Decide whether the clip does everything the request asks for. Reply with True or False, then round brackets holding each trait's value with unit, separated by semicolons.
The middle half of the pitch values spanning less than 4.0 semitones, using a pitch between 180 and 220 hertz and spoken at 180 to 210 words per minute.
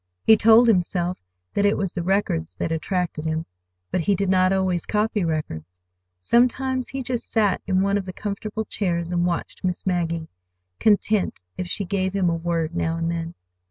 True (3.4 semitones; 185 Hz; 185 wpm)